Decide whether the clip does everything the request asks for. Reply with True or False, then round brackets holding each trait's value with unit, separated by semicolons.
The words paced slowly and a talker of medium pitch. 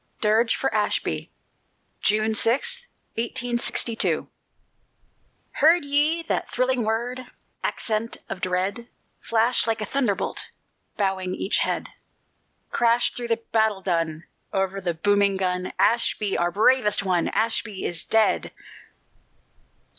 False (110 wpm; 220 Hz)